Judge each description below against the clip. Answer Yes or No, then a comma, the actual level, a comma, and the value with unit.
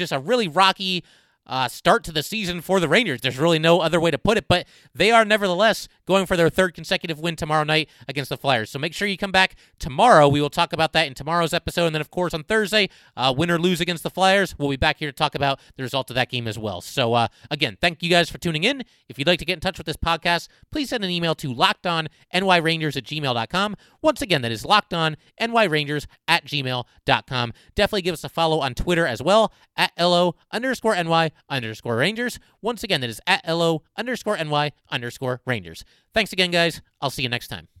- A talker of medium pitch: Yes, medium, 165 Hz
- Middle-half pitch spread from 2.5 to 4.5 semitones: No, average, 5.0 semitones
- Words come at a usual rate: No, fast, 230 wpm